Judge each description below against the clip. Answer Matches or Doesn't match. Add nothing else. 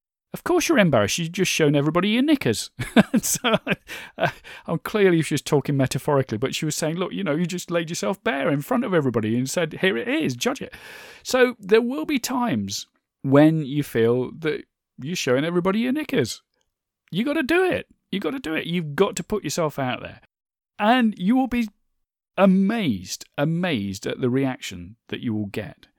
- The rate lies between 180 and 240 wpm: Matches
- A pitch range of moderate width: Doesn't match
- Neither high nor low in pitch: Matches